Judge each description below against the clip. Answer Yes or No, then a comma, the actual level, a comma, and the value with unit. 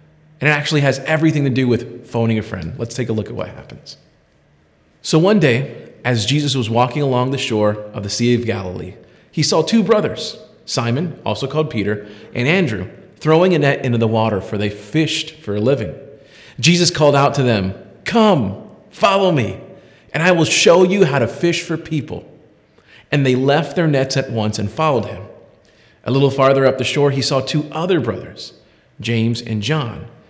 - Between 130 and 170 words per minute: No, average, 190 wpm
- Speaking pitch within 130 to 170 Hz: Yes, low, 135 Hz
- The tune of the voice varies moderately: No, wide, 5.7 semitones